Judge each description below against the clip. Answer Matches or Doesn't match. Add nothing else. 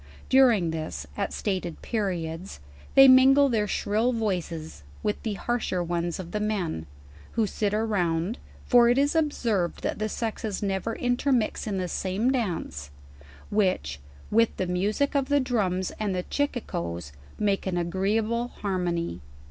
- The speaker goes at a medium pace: Matches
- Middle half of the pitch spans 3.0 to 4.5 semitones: Doesn't match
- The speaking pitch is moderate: Doesn't match